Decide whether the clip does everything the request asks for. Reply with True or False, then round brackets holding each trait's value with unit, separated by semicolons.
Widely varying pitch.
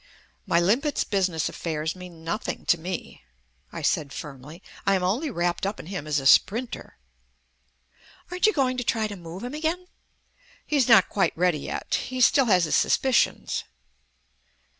True (7.1 semitones)